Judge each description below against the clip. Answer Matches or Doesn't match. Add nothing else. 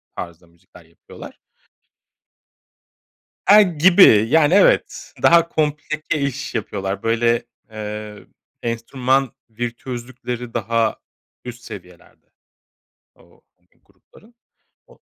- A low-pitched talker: Matches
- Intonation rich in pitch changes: Matches